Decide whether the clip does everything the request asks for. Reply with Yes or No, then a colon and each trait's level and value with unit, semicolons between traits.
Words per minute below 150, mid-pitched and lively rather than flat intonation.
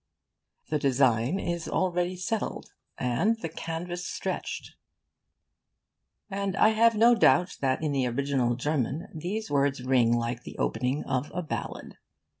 Yes: slow, 135 wpm; medium, 155 Hz; wide, 5.9 semitones